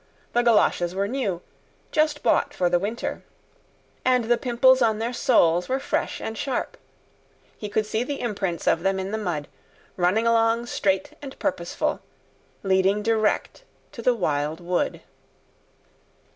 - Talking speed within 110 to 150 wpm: Yes, average, 145 wpm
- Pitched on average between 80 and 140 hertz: No, high, 220 Hz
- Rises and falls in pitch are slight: No, average, 4.2 semitones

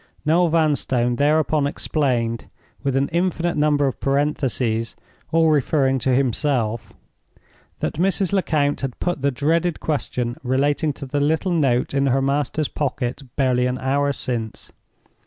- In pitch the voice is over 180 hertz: No, medium, 140 Hz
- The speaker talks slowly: Yes, slow, 130 wpm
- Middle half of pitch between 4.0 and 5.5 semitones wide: No, average, 3.3 semitones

